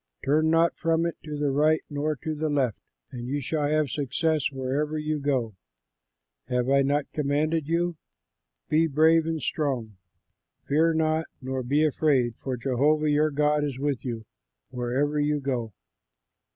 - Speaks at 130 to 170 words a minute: Yes, average, 155 wpm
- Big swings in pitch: No, average, 2.7 semitones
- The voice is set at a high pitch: No, medium, 145 Hz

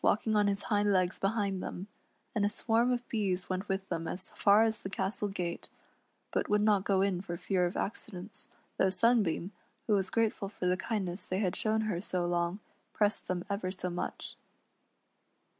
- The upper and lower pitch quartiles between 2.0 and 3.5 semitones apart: Yes, narrow, 2.5 semitones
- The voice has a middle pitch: No, high, 195 Hz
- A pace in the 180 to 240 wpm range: Yes, average, 190 wpm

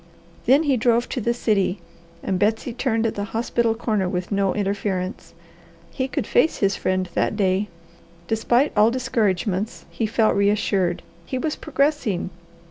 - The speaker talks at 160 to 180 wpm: No, average, 150 wpm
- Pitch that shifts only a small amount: No, average, 3.5 semitones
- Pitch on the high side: Yes, high, 215 Hz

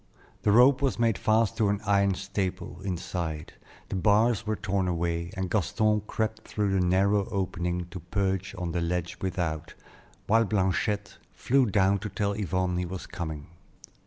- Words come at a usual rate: Yes, average, 160 wpm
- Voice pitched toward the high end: No, very low, 95 Hz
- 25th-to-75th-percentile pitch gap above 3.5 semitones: No, average, 3.0 semitones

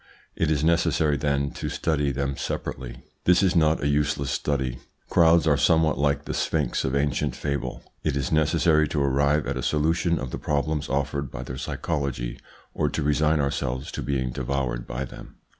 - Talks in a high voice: No, very low, 70 Hz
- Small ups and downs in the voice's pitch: Yes, narrow, 2.3 semitones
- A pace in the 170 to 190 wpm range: Yes, average, 180 wpm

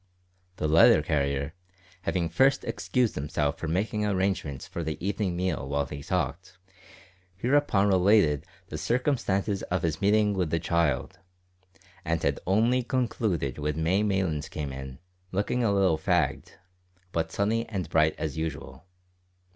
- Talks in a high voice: No, very low, 90 Hz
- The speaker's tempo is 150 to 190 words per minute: No, average, 140 wpm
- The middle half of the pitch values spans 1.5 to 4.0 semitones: No, average, 4.9 semitones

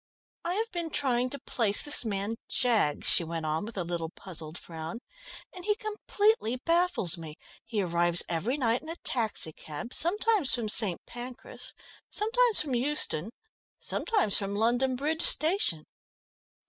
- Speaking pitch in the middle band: No, high, 240 Hz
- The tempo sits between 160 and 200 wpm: No, average, 145 wpm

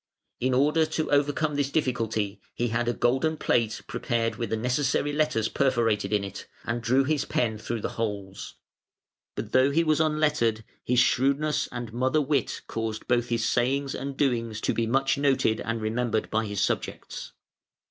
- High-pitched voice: No, low, 120 Hz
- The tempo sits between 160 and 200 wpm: Yes, average, 170 wpm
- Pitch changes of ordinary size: Yes, average, 3.8 semitones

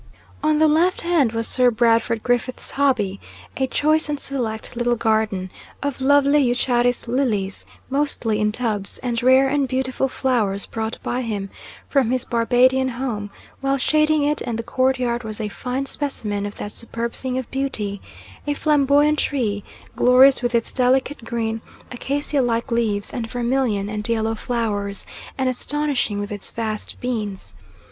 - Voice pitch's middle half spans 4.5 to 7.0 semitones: No, average, 3.5 semitones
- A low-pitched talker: No, high, 245 Hz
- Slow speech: No, average, 155 wpm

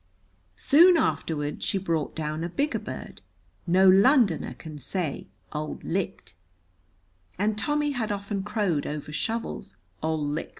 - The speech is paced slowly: Yes, slow, 130 wpm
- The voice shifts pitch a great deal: Yes, wide, 6.3 semitones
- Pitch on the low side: No, medium, 185 Hz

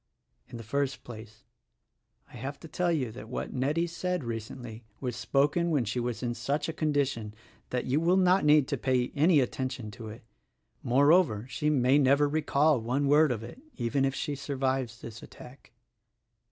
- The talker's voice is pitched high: No, low, 135 Hz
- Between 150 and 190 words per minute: Yes, average, 180 wpm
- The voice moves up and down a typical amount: Yes, average, 3.6 semitones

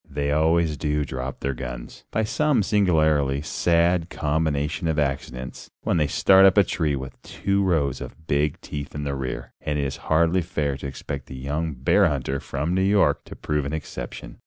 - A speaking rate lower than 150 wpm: No, average, 190 wpm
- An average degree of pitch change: Yes, average, 3.4 semitones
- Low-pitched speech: Yes, very low, 75 Hz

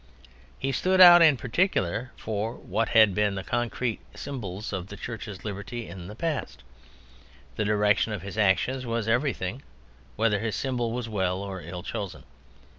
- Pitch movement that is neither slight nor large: Yes, average, 3.8 semitones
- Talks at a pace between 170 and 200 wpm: No, average, 160 wpm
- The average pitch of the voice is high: No, low, 110 Hz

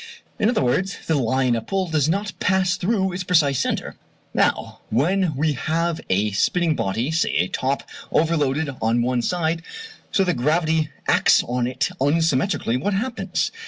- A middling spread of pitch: No, wide, 5.7 semitones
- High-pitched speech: No, medium, 160 Hz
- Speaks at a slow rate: No, average, 160 wpm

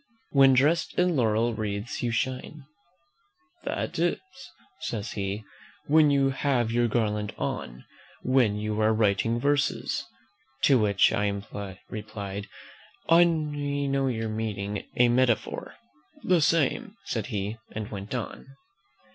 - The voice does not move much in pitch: No, average, 4.7 semitones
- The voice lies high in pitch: No, low, 115 Hz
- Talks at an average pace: No, slow, 120 wpm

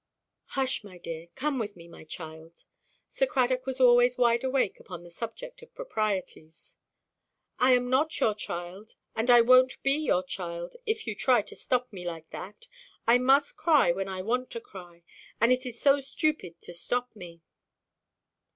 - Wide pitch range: Yes, wide, 6.4 semitones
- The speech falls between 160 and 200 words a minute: Yes, average, 175 wpm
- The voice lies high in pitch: Yes, high, 235 Hz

